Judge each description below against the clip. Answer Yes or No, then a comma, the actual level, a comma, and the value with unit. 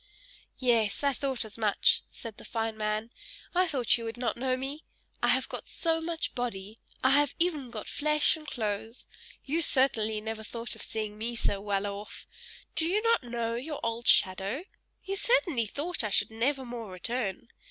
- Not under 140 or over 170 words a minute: No, average, 185 wpm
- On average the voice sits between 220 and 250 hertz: Yes, high, 235 Hz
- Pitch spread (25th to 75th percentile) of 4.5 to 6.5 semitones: Yes, average, 4.9 semitones